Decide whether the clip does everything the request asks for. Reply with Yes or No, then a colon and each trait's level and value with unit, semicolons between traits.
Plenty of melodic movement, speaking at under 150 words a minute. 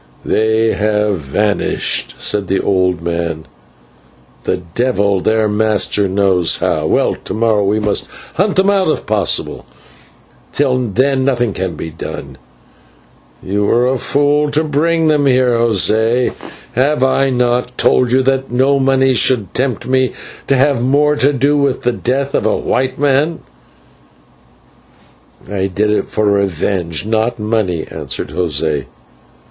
No: average, 4.9 semitones; average, 140 wpm